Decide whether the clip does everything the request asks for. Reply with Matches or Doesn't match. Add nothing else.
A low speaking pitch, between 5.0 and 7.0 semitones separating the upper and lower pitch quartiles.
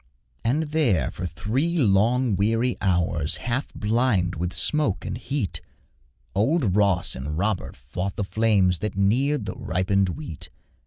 Matches